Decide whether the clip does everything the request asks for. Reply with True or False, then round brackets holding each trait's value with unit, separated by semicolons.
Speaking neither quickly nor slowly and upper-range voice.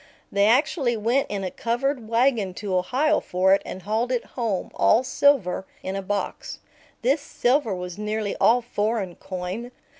True (160 wpm; 220 Hz)